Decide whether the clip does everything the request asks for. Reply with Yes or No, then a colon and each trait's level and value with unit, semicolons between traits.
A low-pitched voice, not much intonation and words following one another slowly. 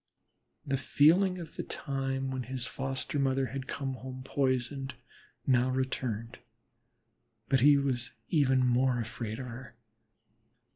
Yes: low, 130 Hz; narrow, 1.4 semitones; slow, 130 wpm